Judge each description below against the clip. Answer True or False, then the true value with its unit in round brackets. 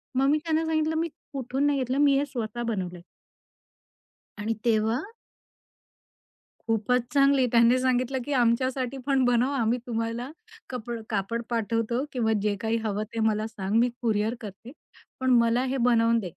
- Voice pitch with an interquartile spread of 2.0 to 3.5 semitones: True (2.8 semitones)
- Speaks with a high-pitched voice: True (235 Hz)